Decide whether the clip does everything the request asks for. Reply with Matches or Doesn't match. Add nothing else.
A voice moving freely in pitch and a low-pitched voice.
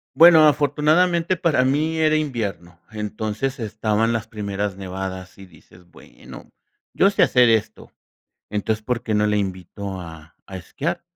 Matches